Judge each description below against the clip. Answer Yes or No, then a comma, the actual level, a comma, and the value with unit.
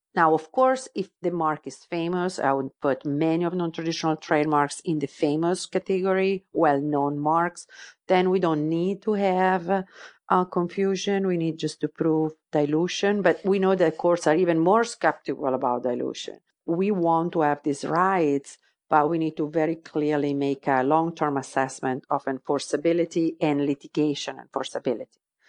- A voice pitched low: No, medium, 165 Hz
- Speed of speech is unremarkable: Yes, average, 160 wpm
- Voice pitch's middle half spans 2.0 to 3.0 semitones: No, average, 3.6 semitones